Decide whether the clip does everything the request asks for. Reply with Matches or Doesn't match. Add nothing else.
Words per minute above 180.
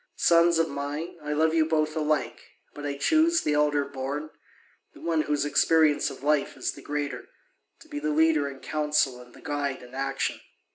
Matches